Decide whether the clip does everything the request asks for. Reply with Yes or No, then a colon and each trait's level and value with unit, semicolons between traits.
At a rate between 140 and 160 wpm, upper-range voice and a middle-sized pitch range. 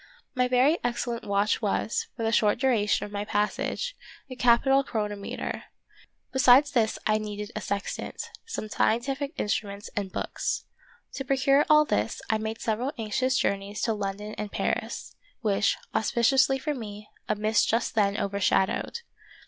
Yes: average, 150 wpm; high, 220 Hz; average, 3.9 semitones